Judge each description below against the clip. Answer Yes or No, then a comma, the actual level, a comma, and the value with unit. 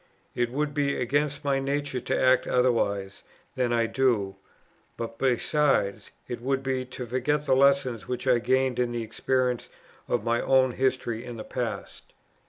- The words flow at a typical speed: Yes, average, 165 wpm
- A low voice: Yes, low, 125 Hz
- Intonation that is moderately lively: No, narrow, 2.2 semitones